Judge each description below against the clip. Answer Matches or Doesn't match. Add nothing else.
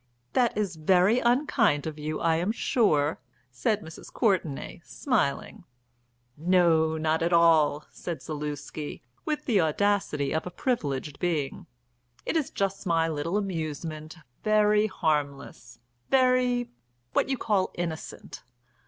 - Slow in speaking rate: Matches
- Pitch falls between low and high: Matches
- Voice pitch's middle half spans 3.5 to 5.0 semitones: Doesn't match